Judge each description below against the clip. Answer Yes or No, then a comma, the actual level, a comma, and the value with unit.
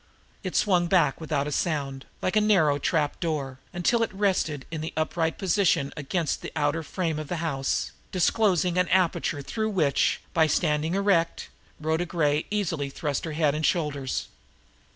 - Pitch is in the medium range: Yes, medium, 160 Hz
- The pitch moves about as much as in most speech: Yes, average, 3.6 semitones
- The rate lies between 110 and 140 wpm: No, average, 165 wpm